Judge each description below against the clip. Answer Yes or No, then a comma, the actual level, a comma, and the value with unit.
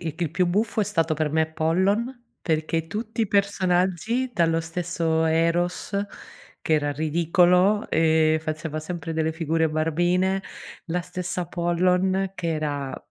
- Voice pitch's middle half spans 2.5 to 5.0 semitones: Yes, average, 2.8 semitones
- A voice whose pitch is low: No, medium, 170 Hz